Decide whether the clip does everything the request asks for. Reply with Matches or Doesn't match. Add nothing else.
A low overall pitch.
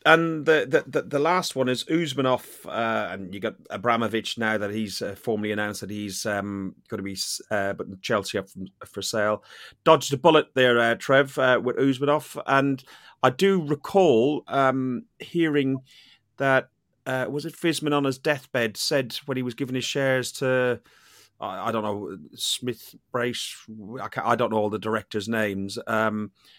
Matches